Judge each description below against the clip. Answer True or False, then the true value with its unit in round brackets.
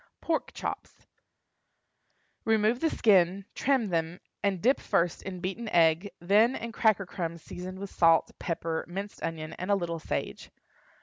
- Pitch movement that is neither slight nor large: True (4.1 semitones)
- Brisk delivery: False (145 wpm)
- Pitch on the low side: False (190 Hz)